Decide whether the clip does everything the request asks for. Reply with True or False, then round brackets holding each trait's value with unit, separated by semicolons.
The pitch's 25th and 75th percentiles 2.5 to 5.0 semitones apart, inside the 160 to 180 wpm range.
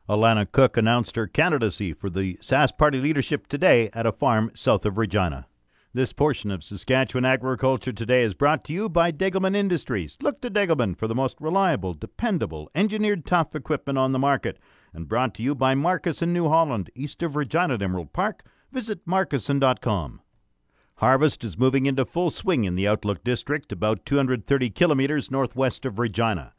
False (5.5 semitones; 175 wpm)